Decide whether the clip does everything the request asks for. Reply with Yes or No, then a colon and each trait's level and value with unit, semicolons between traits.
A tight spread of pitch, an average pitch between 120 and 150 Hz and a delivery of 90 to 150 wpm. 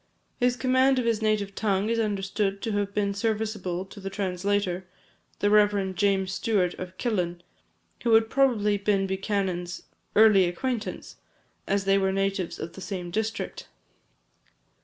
No: narrow, 2.3 semitones; high, 200 Hz; average, 145 wpm